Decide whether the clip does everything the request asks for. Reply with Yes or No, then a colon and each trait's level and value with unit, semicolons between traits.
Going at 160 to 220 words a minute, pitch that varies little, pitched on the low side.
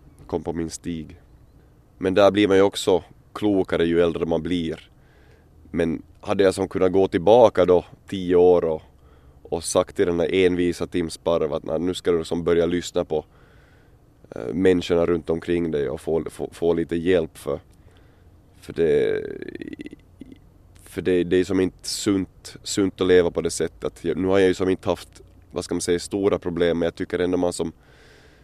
Yes: average, 190 wpm; narrow, 2.0 semitones; very low, 90 Hz